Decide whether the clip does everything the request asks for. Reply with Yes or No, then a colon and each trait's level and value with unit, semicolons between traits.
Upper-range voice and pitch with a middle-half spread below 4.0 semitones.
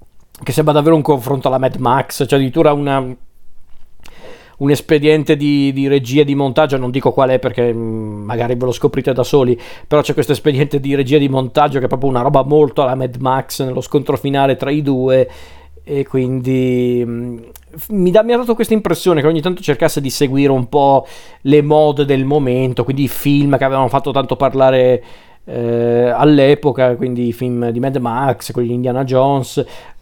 No: low, 135 Hz; narrow, 2.5 semitones